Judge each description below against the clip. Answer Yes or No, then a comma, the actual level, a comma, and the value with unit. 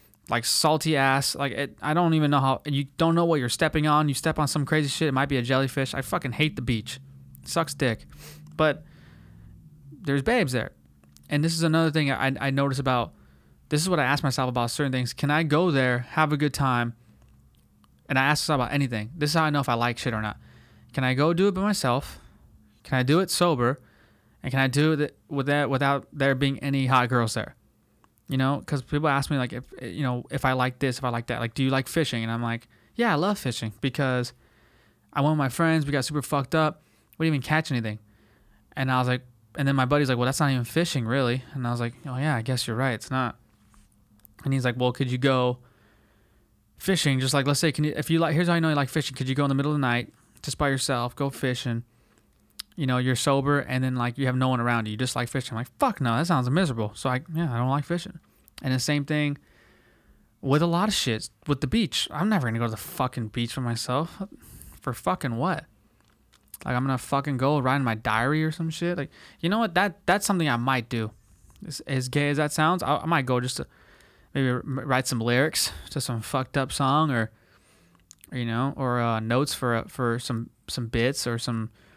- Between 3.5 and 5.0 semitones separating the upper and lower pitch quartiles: Yes, average, 3.8 semitones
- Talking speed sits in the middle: No, fast, 245 wpm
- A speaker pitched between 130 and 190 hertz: Yes, low, 135 Hz